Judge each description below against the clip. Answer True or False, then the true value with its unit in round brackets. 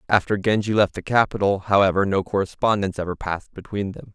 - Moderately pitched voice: False (100 Hz)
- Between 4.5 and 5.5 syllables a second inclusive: False (6.3 syllables/s)